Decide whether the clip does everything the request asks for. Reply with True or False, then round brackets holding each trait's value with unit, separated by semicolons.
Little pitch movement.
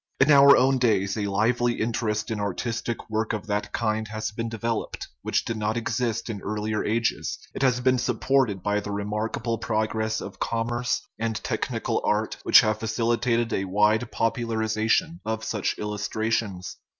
True (1.9 semitones)